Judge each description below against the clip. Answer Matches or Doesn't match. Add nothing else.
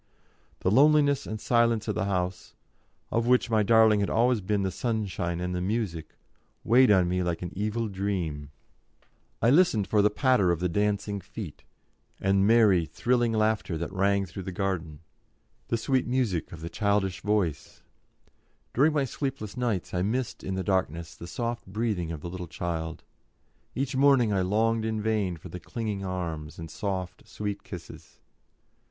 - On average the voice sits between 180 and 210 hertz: Doesn't match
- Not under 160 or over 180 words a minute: Matches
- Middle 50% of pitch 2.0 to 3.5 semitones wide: Doesn't match